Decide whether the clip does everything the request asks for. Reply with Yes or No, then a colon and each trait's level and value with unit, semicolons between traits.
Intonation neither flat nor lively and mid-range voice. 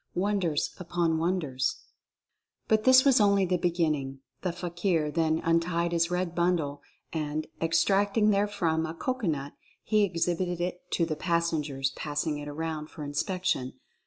Yes: average, 3.0 semitones; medium, 170 Hz